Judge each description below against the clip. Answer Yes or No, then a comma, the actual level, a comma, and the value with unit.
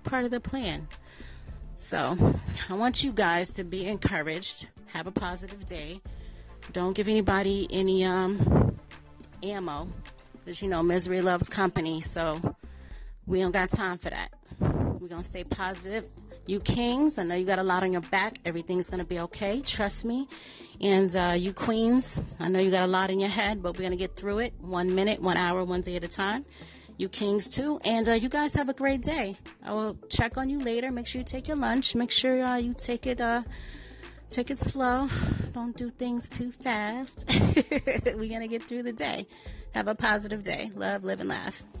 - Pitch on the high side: Yes, high, 195 Hz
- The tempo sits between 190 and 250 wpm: Yes, average, 200 wpm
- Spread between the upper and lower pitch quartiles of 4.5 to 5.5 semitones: Yes, average, 5.1 semitones